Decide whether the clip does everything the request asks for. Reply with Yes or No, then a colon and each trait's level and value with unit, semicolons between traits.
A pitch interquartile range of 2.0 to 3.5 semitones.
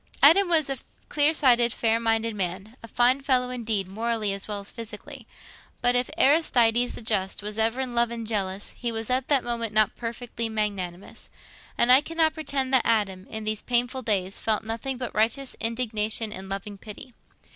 Yes: average, 3.0 semitones